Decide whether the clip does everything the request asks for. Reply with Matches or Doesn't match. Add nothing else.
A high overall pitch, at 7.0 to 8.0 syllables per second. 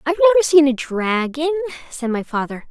Matches